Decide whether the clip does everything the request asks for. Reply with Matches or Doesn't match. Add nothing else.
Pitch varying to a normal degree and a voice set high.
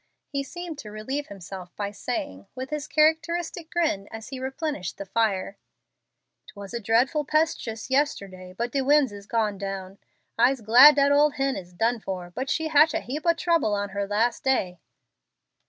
Doesn't match